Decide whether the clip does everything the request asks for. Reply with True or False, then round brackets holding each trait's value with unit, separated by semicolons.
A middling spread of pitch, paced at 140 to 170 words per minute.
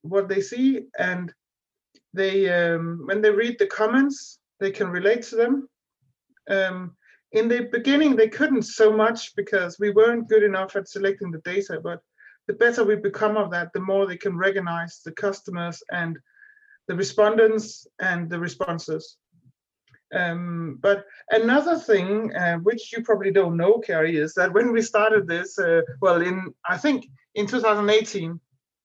True (3.9 semitones; 160 wpm)